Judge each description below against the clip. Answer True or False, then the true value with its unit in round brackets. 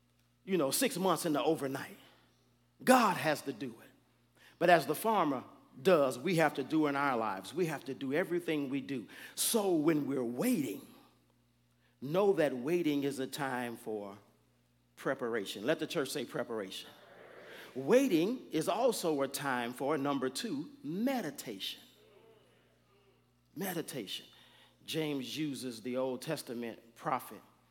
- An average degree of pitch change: True (4.8 semitones)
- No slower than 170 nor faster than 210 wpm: False (140 wpm)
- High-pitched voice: False (140 Hz)